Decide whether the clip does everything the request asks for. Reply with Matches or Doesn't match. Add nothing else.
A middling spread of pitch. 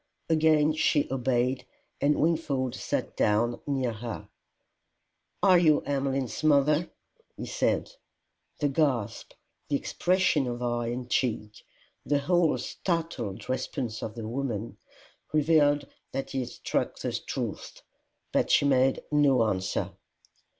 Matches